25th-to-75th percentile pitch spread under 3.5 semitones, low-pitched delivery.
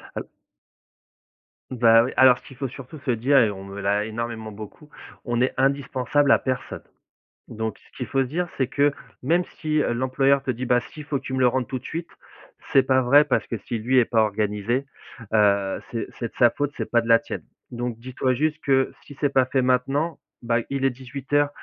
Yes: average, 2.9 semitones; low, 130 Hz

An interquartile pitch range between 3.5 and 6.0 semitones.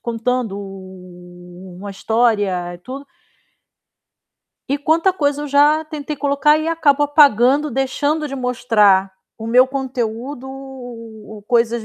Yes: average, 4.8 semitones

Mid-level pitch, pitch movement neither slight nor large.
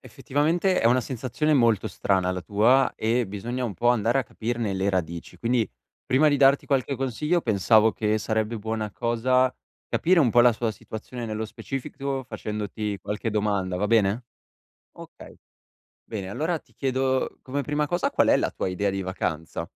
No: low, 115 Hz; average, 4.1 semitones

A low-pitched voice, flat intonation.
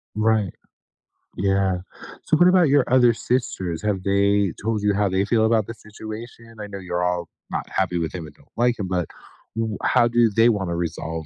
No: low, 105 Hz; average, 3.6 semitones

